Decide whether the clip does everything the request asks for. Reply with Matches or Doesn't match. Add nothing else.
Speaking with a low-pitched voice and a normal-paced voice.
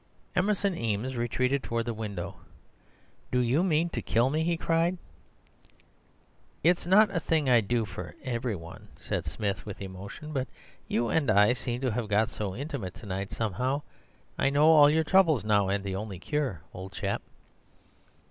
Matches